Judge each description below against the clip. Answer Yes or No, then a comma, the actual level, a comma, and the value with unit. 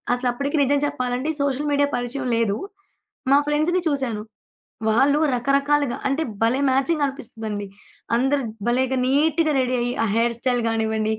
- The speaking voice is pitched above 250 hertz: Yes, very high, 260 Hz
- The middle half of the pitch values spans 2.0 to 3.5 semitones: Yes, average, 3.1 semitones